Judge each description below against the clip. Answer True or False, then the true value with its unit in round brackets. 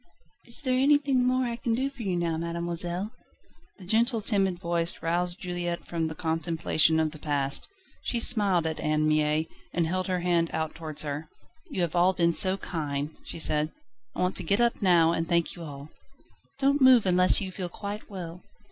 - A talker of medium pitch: True (175 Hz)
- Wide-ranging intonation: False (4.0 semitones)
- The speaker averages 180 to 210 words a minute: True (190 wpm)